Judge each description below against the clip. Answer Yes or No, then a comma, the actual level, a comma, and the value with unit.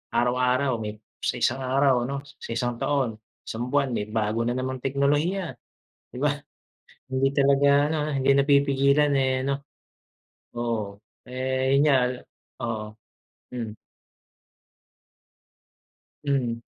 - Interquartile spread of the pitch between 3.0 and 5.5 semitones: No, narrow, 2.6 semitones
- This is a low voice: Yes, low, 130 Hz